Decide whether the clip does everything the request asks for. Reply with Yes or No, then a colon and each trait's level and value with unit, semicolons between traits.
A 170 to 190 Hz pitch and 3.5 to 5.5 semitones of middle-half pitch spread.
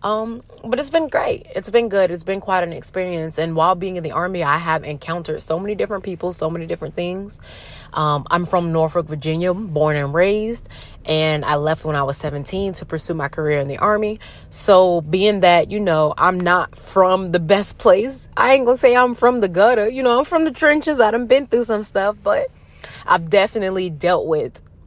Yes: medium, 185 Hz; average, 5.0 semitones